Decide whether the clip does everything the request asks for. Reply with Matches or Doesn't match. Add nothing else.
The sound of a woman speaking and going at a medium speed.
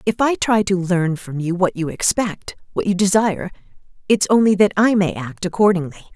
Matches